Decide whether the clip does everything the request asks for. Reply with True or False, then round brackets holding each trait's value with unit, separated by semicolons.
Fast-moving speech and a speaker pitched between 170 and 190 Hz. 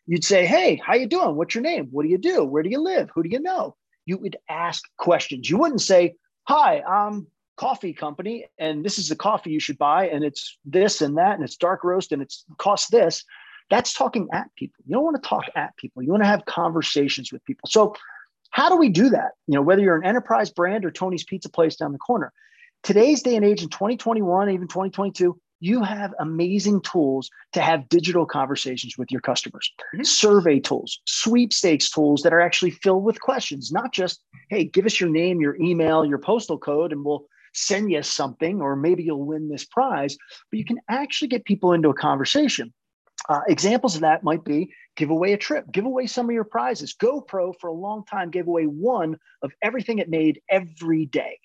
True (210 wpm; 185 Hz)